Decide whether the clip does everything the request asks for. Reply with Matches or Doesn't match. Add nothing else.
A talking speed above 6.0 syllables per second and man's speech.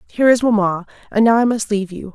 Doesn't match